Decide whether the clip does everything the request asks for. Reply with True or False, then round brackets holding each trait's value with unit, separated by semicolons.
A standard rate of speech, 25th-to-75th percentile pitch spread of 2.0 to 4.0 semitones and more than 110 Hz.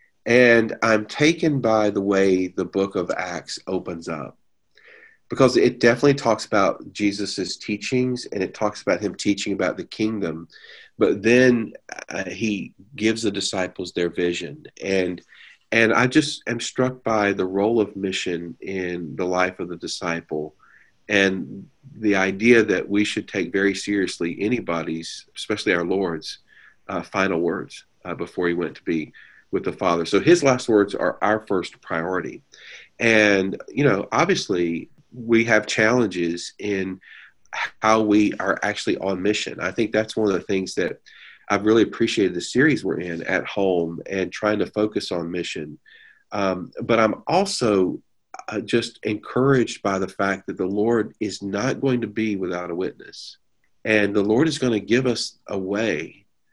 False (165 wpm; 3.4 semitones; 105 Hz)